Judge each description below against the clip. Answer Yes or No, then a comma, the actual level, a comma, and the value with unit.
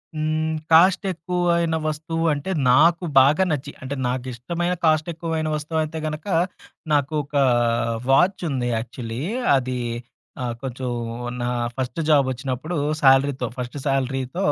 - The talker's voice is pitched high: No, medium, 150 Hz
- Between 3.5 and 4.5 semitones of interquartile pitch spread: Yes, average, 3.9 semitones